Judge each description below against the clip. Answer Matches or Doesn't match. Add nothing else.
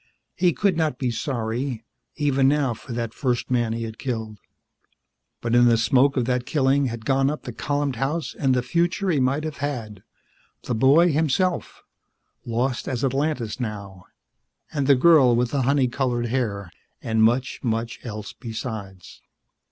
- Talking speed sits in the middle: Matches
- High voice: Doesn't match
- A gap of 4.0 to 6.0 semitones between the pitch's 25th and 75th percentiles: Doesn't match